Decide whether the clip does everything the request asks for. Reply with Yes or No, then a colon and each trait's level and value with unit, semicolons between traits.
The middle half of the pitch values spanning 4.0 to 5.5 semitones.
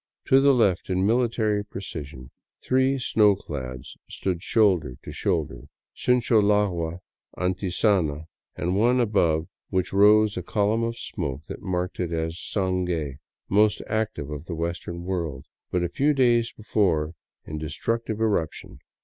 Yes: average, 4.8 semitones